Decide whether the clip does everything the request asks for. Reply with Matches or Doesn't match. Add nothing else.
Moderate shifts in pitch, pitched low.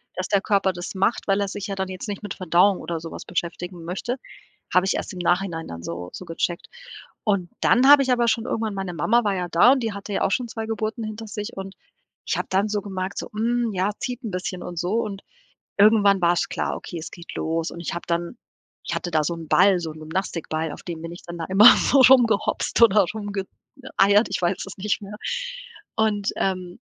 Doesn't match